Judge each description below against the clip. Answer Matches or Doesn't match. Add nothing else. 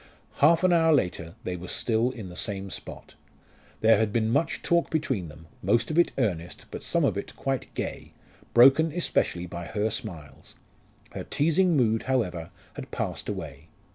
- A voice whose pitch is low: Matches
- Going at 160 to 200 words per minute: Matches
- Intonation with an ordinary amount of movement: Doesn't match